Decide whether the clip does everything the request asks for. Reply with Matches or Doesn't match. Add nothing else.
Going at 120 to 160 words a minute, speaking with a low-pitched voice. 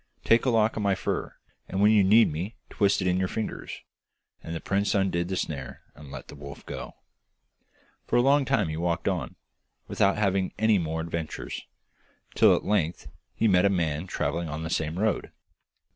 Doesn't match